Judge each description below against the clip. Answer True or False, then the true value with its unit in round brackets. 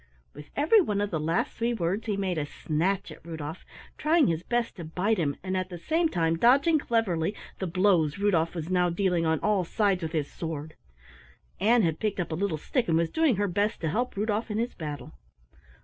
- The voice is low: False (185 Hz)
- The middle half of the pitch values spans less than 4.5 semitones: False (5.0 semitones)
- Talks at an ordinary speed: False (215 wpm)